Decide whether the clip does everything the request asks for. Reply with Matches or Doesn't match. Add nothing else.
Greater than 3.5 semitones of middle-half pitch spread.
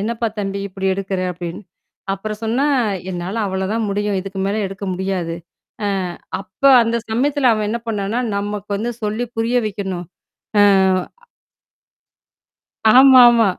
Doesn't match